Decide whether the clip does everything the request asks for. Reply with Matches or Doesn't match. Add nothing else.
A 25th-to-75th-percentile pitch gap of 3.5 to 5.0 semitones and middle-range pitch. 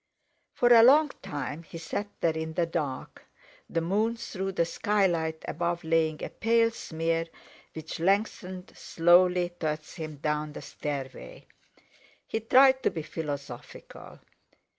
Matches